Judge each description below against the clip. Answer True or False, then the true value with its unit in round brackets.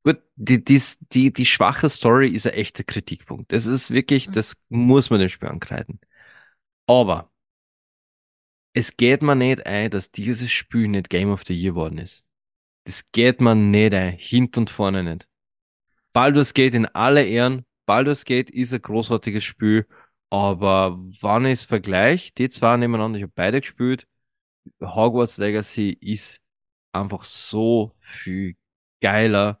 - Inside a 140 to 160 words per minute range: True (150 wpm)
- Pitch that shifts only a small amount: False (4.2 semitones)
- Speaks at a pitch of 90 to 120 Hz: True (110 Hz)